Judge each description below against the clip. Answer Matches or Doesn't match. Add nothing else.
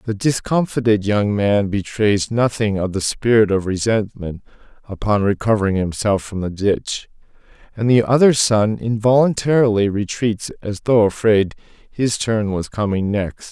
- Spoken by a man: Matches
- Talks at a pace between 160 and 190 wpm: Doesn't match